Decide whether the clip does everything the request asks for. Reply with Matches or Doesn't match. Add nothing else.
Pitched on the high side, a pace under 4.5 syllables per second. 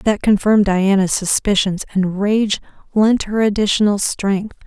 Matches